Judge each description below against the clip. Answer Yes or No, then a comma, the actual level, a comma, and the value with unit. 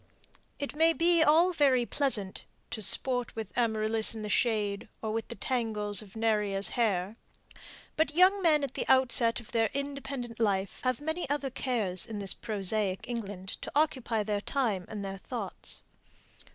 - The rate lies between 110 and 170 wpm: Yes, average, 165 wpm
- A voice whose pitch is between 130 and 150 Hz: No, high, 230 Hz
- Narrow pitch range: No, average, 5.1 semitones